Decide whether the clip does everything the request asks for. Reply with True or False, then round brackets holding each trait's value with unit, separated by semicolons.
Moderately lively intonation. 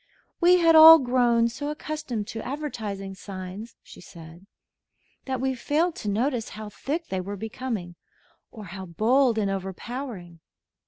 False (5.7 semitones)